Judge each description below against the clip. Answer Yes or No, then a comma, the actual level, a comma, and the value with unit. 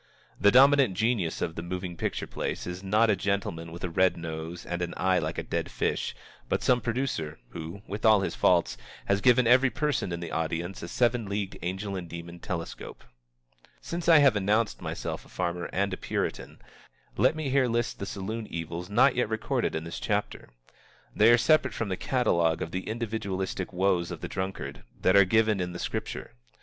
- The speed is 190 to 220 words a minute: Yes, average, 195 wpm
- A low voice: Yes, very low, 95 Hz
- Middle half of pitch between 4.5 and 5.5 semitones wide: Yes, average, 4.8 semitones